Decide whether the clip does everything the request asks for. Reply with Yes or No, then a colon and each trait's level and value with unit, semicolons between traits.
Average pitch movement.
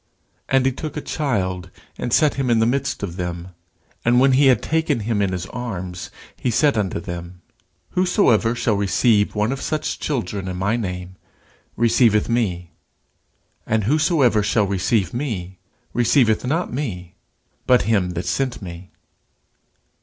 No: wide, 5.9 semitones